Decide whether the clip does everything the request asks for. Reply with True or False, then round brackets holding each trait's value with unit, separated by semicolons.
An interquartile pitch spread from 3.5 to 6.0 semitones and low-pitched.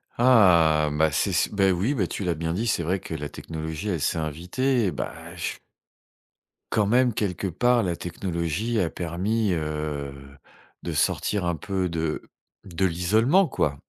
True (4.7 semitones; 90 Hz)